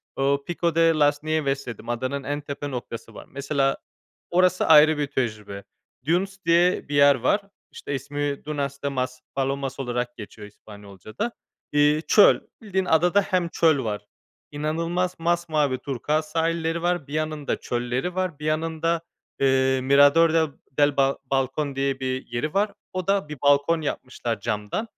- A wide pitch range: No, average, 3.8 semitones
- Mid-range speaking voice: Yes, medium, 145 Hz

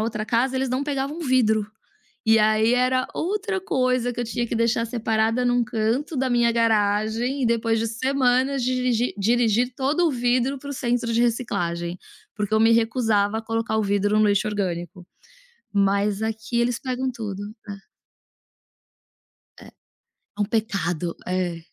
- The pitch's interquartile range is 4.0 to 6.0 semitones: No, average, 2.9 semitones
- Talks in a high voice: Yes, high, 230 Hz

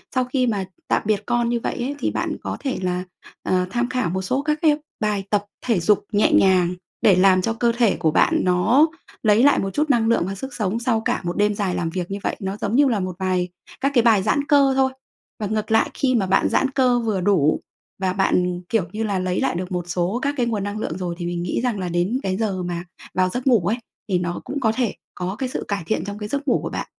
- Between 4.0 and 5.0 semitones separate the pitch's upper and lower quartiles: Yes, average, 4.7 semitones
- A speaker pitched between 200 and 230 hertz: Yes, high, 205 Hz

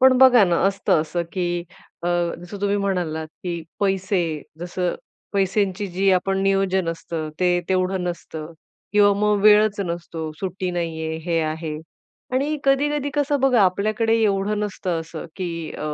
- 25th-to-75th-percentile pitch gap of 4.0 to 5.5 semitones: No, average, 3.2 semitones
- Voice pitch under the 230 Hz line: Yes, high, 190 Hz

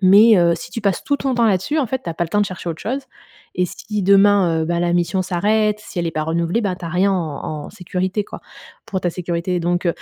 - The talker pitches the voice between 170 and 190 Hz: Yes, medium, 185 Hz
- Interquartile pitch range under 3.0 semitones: No, average, 3.3 semitones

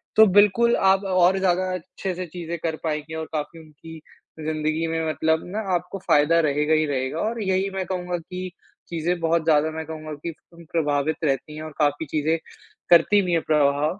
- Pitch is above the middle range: No, medium, 165 Hz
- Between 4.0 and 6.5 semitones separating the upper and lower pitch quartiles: No, average, 2.9 semitones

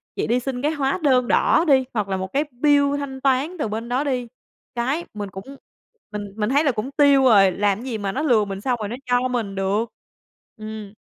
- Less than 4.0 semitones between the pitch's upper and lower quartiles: No, average, 4.6 semitones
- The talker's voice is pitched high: Yes, high, 245 Hz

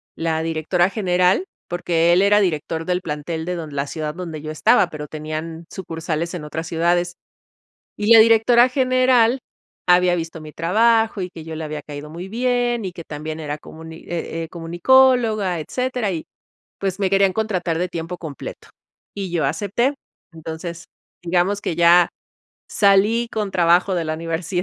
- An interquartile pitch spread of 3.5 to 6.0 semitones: Yes, average, 3.8 semitones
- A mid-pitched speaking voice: Yes, medium, 175 Hz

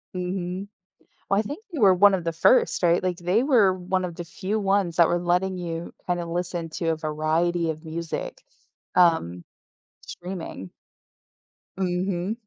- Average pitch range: No, narrow, 2.1 semitones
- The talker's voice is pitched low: No, medium, 180 Hz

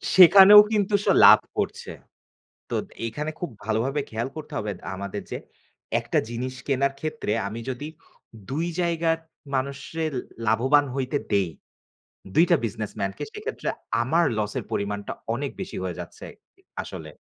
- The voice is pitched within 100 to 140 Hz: Yes, low, 135 Hz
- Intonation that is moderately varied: No, wide, 6.9 semitones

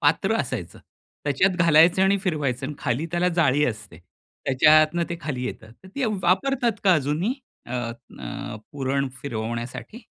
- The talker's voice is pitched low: No, medium, 150 Hz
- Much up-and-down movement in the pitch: Yes, wide, 5.8 semitones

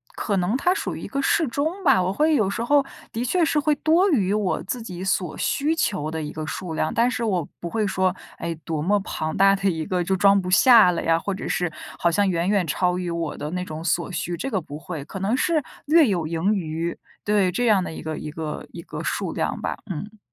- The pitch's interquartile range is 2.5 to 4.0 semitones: No, wide, 5.5 semitones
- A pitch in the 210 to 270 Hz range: No, high, 190 Hz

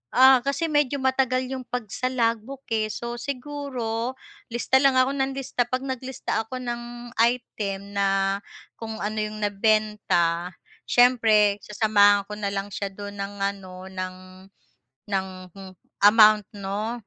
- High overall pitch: Yes, high, 220 Hz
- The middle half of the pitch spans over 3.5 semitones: Yes, average, 4.1 semitones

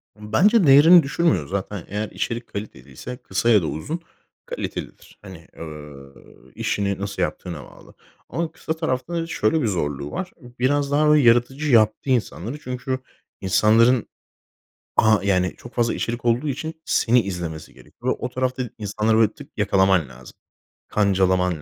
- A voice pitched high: No, low, 110 Hz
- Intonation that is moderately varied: No, wide, 5.7 semitones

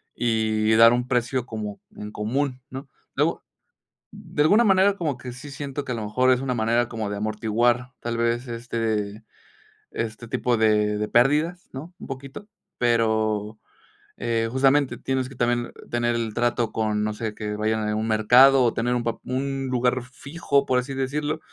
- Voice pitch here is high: No, low, 120 Hz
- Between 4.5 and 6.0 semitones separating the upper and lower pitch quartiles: No, average, 3.2 semitones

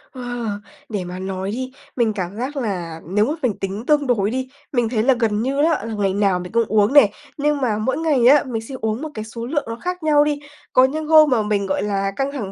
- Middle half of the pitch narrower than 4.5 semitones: No, average, 5.2 semitones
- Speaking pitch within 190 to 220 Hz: No, high, 230 Hz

